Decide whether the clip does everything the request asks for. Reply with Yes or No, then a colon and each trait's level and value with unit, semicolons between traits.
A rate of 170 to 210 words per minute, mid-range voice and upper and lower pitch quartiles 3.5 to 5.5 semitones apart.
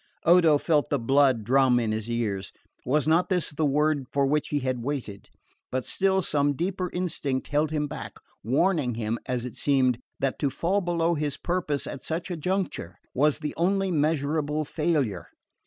Yes: average, 175 wpm; medium, 145 Hz; average, 4.2 semitones